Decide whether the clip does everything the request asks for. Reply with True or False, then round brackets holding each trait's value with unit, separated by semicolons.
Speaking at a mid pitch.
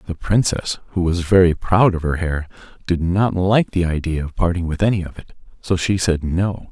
False (90 Hz)